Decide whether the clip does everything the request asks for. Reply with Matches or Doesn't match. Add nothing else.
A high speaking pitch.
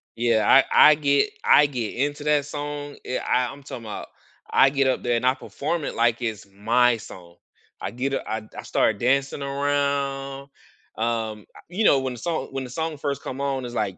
Doesn't match